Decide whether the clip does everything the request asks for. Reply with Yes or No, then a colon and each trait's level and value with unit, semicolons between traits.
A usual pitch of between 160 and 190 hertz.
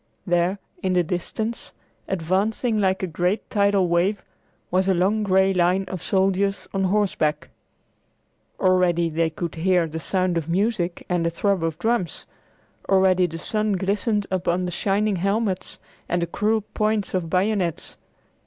Yes: medium, 185 Hz